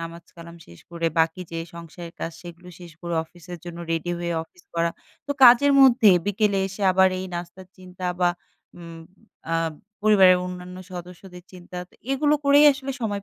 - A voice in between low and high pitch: Yes, medium, 180 Hz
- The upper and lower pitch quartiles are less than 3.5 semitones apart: Yes, average, 2.8 semitones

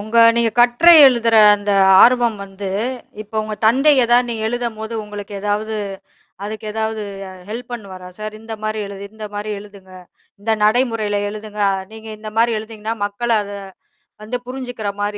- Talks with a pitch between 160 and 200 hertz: No, high, 220 Hz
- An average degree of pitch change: No, narrow, 2.2 semitones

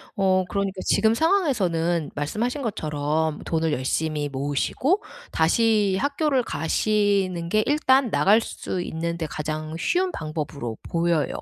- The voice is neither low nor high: Yes, medium, 175 Hz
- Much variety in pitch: Yes, wide, 6.4 semitones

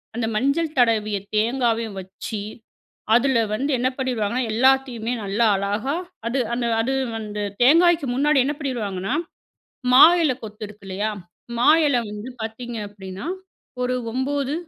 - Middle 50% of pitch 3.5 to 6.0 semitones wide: Yes, average, 3.9 semitones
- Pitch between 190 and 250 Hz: Yes, high, 235 Hz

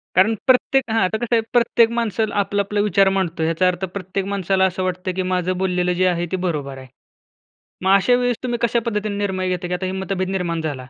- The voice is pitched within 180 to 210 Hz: Yes, high, 190 Hz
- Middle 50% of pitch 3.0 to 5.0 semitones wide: No, narrow, 2.6 semitones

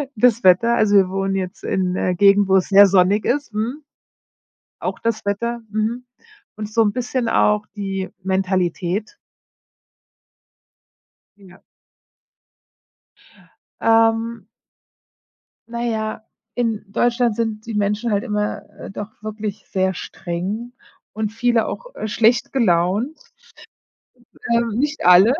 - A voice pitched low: No, high, 215 Hz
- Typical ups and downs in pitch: Yes, average, 3.2 semitones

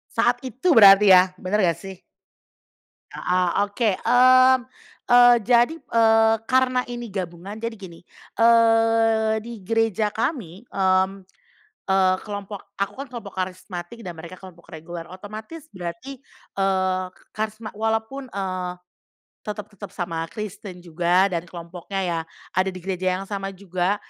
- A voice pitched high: Yes, high, 200 Hz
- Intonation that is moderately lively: Yes, average, 3.6 semitones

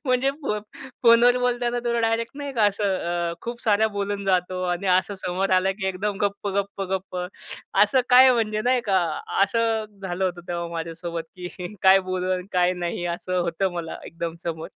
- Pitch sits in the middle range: No, high, 195 Hz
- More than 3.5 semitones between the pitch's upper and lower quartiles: Yes, average, 4.2 semitones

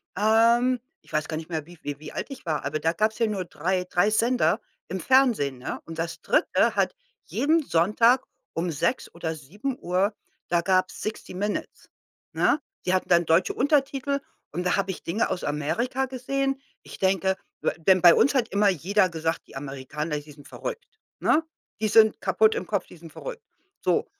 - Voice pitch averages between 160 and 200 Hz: Yes, high, 190 Hz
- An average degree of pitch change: No, wide, 6.5 semitones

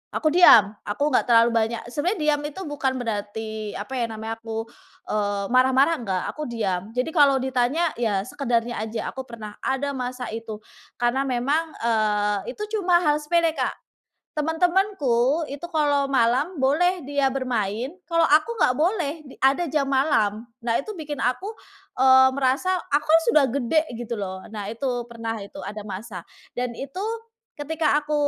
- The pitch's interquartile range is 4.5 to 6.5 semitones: Yes, average, 5.0 semitones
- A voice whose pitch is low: No, very high, 260 Hz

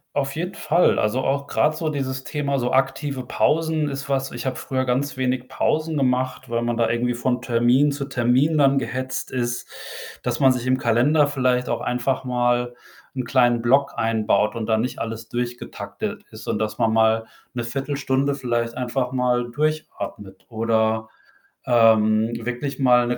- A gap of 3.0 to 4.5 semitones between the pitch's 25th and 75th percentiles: No, narrow, 2.5 semitones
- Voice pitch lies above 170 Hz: No, low, 125 Hz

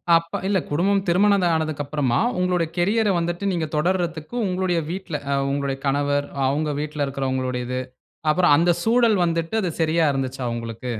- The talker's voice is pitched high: No, medium, 160 Hz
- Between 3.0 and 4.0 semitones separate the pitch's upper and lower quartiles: No, average, 4.5 semitones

